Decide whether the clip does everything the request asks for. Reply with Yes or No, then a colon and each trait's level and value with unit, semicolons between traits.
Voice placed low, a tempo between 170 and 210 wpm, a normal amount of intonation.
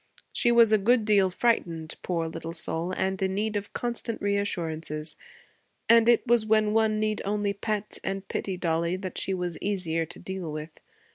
No: high, 195 Hz; average, 180 wpm; average, 4.2 semitones